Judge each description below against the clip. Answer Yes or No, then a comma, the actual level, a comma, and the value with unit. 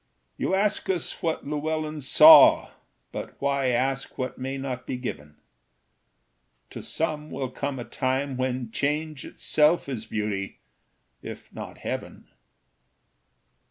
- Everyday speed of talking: No, slow, 125 wpm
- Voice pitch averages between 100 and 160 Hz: Yes, low, 135 Hz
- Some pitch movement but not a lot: Yes, average, 3.1 semitones